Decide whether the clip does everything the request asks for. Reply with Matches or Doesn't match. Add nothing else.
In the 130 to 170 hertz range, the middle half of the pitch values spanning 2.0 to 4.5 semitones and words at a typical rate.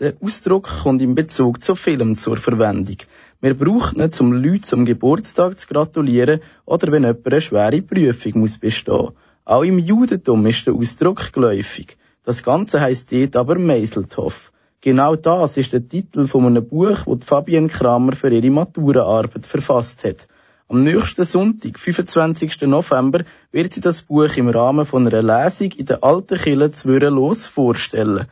Doesn't match